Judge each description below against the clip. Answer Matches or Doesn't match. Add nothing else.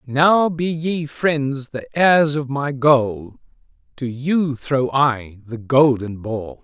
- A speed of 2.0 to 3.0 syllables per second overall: Matches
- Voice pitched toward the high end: Doesn't match